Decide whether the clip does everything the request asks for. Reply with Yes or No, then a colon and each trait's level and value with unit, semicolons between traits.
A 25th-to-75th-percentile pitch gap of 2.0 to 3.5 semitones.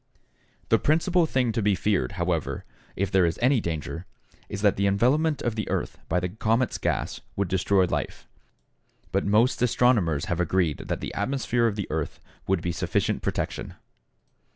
No: average, 5.1 semitones